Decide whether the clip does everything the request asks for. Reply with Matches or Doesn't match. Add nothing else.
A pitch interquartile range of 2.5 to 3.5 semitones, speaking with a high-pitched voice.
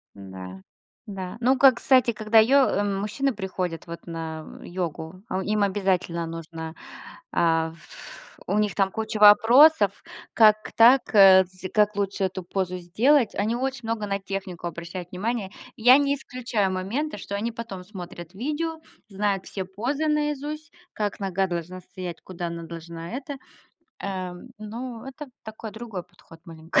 Doesn't match